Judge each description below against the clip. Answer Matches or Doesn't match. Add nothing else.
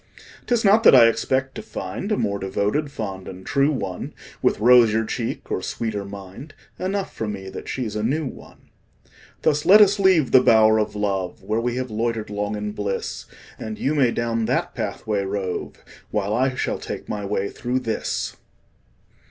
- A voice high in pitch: Doesn't match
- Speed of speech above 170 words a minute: Matches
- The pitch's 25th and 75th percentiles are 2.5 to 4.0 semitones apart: Doesn't match